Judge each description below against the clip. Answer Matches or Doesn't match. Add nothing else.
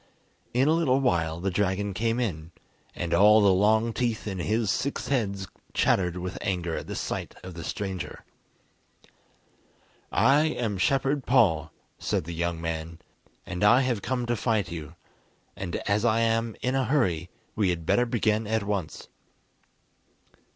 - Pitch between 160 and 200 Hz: Doesn't match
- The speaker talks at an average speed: Matches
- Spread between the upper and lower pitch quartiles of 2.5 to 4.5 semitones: Doesn't match